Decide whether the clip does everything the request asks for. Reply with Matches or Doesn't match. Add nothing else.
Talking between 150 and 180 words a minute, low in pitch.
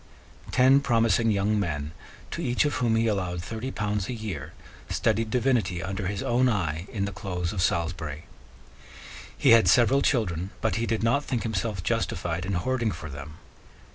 Matches